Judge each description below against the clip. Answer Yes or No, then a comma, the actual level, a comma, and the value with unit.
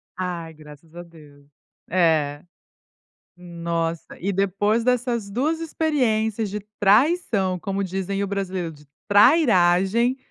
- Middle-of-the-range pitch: No, high, 195 Hz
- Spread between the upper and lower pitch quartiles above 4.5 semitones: Yes, average, 4.9 semitones